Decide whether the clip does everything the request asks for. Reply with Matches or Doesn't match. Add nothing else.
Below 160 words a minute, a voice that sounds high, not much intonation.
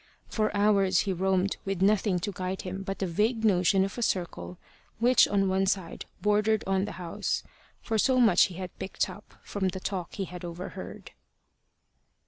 Doesn't match